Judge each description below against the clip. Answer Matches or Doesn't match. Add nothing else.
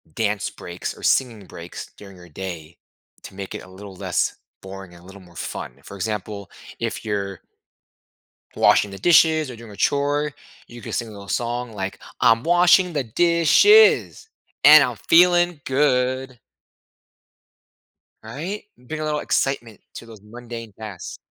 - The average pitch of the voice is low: Matches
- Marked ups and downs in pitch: Matches